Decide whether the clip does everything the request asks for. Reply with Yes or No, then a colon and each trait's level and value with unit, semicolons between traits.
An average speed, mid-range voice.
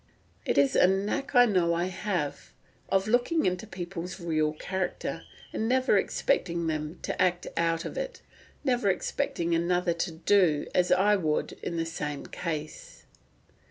Yes: average, 150 wpm; medium, 180 Hz